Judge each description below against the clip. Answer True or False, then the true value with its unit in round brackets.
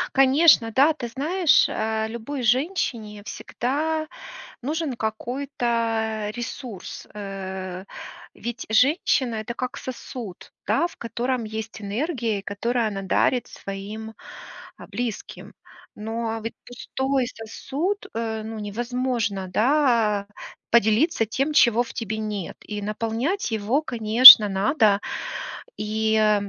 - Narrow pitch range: False (3.4 semitones)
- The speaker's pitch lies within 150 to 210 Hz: False (230 Hz)